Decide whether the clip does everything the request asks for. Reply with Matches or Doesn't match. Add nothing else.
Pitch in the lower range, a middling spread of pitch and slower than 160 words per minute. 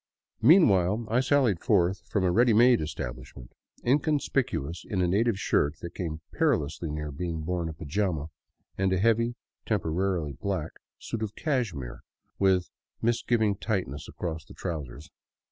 Doesn't match